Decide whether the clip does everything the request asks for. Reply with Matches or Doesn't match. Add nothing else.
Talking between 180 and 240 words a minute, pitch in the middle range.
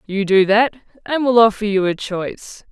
Doesn't match